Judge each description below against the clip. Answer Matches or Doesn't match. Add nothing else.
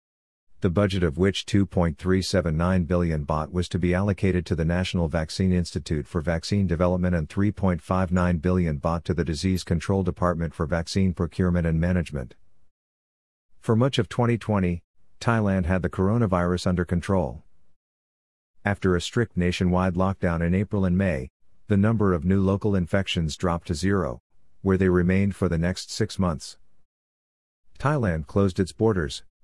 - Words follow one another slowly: Doesn't match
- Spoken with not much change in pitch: Matches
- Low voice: Matches